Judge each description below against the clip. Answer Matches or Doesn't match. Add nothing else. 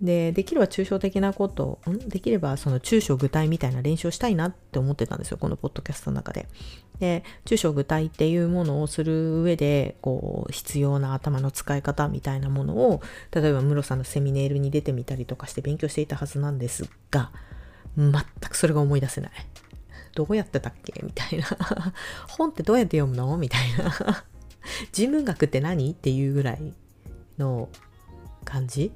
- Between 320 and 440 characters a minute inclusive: Matches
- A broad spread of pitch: Doesn't match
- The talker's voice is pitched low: Doesn't match